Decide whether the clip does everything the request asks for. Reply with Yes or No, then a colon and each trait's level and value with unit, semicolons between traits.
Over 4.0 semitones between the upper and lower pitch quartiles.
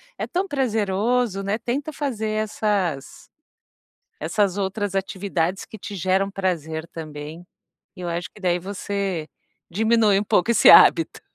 No: average, 3.5 semitones